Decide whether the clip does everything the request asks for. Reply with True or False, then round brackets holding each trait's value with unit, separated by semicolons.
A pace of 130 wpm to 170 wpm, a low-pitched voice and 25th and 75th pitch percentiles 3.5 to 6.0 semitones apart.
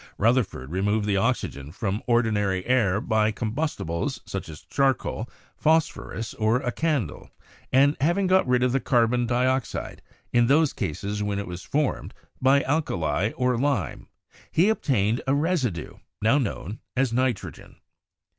True (145 wpm; 120 Hz; 4.8 semitones)